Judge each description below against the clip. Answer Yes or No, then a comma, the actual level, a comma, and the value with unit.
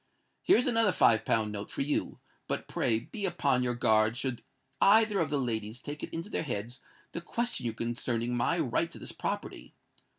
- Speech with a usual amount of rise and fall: No, wide, 7.0 semitones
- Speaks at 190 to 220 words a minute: Yes, average, 195 wpm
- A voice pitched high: No, low, 125 Hz